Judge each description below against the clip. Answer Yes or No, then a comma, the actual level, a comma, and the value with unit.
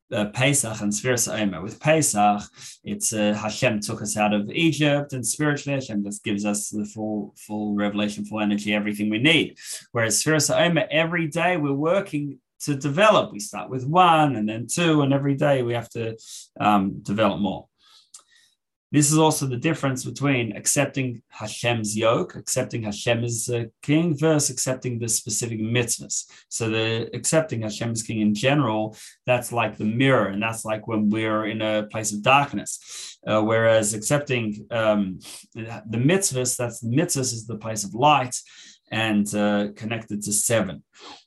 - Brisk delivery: No, average, 165 wpm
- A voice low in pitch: Yes, low, 115 Hz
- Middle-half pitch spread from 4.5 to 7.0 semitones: Yes, average, 4.8 semitones